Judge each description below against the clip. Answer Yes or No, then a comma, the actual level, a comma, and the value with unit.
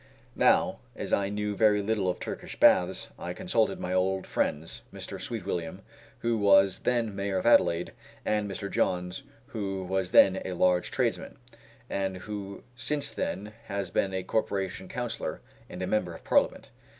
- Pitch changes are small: Yes, narrow, 2.1 semitones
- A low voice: Yes, very low, 95 Hz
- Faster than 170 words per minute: No, average, 160 wpm